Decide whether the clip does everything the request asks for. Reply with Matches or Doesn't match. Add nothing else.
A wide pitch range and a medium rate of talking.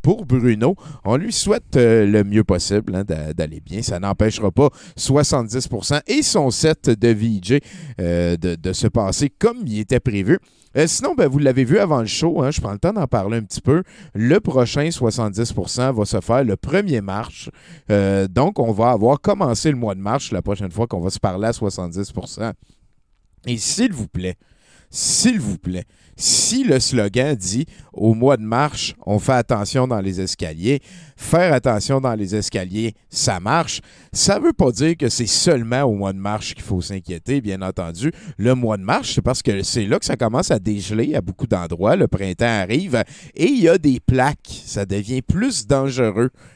Matches